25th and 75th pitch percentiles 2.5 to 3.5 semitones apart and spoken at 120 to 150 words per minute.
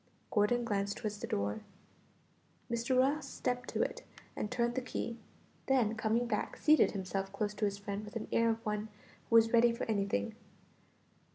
No: average, 2.8 semitones; average, 175 wpm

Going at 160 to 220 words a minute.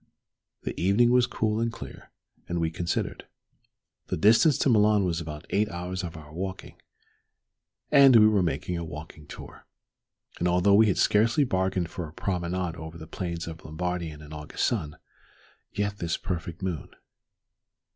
Yes: average, 165 wpm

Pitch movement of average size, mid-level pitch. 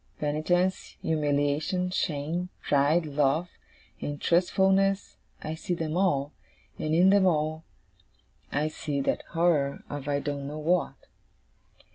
Yes: average, 3.5 semitones; medium, 155 Hz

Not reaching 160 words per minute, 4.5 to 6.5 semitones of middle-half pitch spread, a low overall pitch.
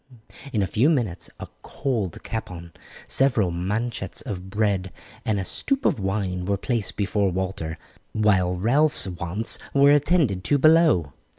Yes: average, 140 wpm; average, 4.9 semitones; low, 100 Hz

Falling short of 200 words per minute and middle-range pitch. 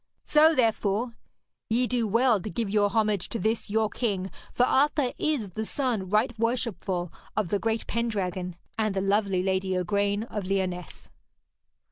No: average, 155 wpm; high, 215 Hz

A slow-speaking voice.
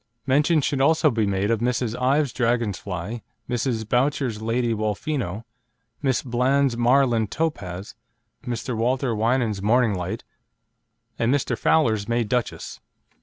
Yes: slow, 125 wpm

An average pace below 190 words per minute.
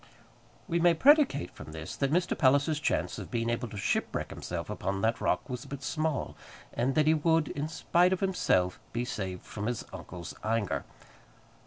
Yes: average, 180 wpm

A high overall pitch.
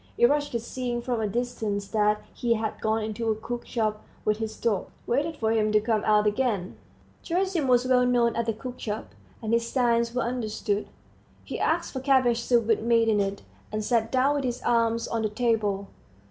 Yes: high, 230 Hz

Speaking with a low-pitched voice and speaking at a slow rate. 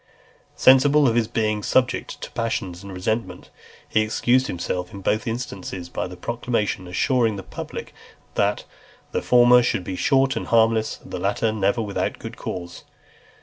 No: low, 110 Hz; average, 165 wpm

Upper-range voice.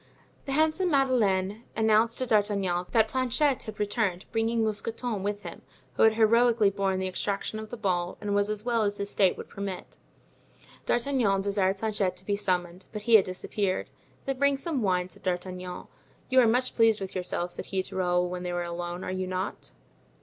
Yes: high, 205 Hz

